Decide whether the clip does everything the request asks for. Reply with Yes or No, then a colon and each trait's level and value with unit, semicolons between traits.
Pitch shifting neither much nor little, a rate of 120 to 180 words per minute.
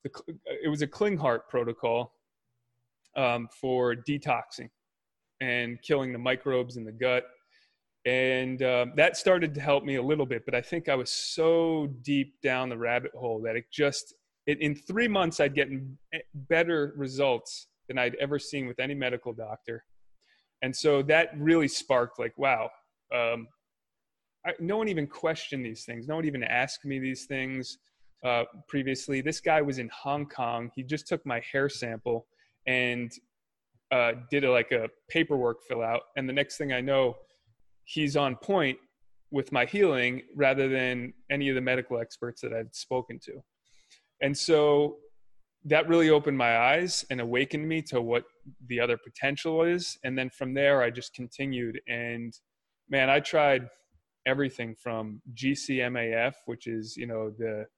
Yes: average, 3.4 semitones; average, 165 wpm